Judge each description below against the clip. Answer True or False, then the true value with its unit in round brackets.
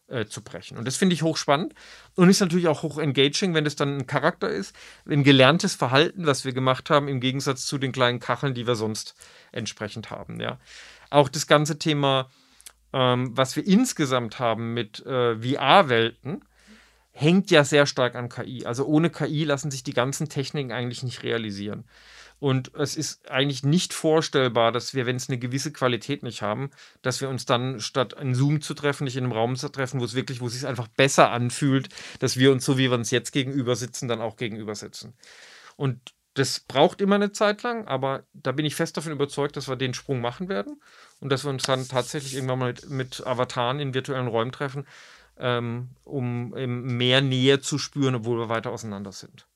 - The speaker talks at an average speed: False (200 wpm)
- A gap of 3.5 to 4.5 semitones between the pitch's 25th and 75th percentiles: False (3.0 semitones)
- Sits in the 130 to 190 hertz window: True (135 Hz)